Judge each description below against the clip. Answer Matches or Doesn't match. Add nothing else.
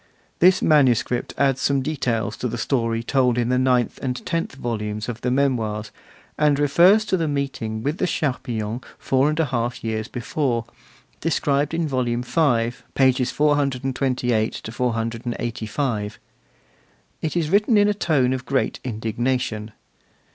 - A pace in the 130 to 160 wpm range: Matches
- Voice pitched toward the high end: Doesn't match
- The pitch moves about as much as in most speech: Matches